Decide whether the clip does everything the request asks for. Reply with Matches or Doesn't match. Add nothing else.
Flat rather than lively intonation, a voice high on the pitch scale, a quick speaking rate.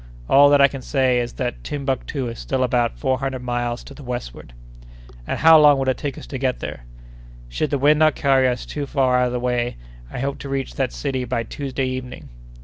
Doesn't match